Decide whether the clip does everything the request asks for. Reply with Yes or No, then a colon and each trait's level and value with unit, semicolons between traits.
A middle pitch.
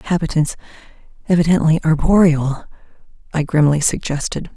Yes: medium, 160 Hz